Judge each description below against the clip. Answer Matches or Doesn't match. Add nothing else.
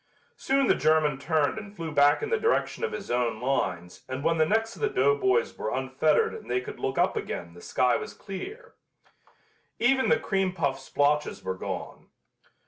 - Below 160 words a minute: Doesn't match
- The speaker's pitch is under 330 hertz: Matches